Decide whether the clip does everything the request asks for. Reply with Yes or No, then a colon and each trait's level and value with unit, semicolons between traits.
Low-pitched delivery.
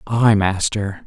Yes: low, 105 Hz